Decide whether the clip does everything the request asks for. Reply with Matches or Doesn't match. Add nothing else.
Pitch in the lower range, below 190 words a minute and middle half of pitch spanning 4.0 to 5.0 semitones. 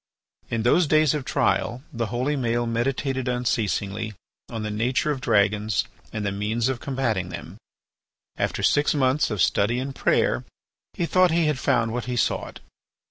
Doesn't match